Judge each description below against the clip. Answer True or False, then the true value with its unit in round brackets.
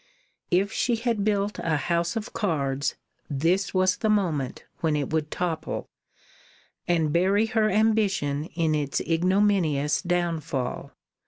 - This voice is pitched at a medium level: True (175 Hz)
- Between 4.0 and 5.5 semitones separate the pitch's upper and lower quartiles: True (4.9 semitones)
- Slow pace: True (130 wpm)